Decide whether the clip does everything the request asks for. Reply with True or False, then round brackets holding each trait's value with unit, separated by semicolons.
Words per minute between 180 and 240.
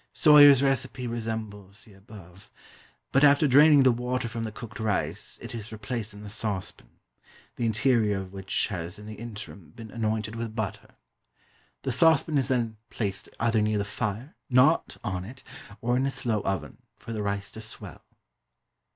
False (170 wpm)